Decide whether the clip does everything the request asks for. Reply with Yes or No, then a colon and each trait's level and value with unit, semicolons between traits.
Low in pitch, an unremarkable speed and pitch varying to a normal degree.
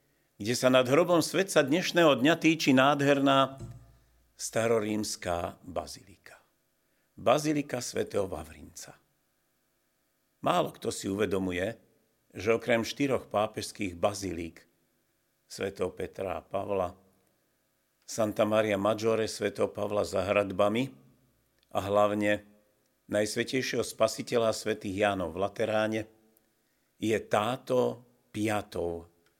No: low, 110 Hz; slow, 90 wpm; average, 3.6 semitones